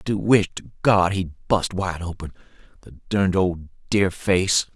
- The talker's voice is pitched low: Yes, very low, 95 Hz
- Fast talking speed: No, average, 175 wpm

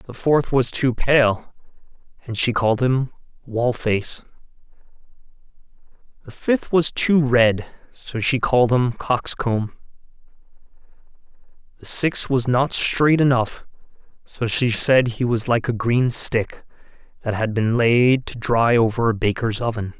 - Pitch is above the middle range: No, low, 120 Hz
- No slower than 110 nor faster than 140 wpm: Yes, slow, 135 wpm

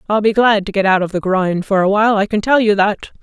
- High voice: Yes, high, 205 Hz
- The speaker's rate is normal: No, fast, 315 wpm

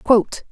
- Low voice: No, high, 220 Hz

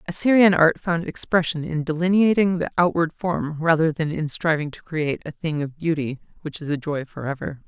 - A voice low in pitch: No, medium, 160 Hz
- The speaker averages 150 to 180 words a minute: No, average, 195 wpm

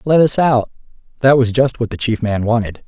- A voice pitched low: Yes, low, 120 Hz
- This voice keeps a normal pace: No, fast, 230 wpm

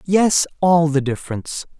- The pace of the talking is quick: No, slow, 135 wpm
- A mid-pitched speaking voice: Yes, medium, 160 Hz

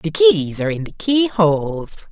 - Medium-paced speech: Yes, average, 170 wpm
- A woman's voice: No, male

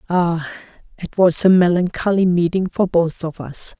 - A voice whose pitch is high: No, medium, 175 Hz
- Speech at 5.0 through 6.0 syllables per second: No, 4.6 syllables/s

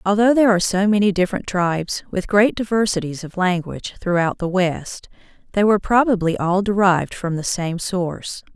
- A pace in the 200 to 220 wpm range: No, average, 170 wpm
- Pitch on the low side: No, high, 190 Hz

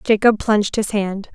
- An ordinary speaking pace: Yes, average, 180 wpm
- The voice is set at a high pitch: Yes, high, 210 Hz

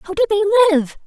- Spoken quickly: Yes, fast, 225 wpm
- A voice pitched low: No, very high, 390 Hz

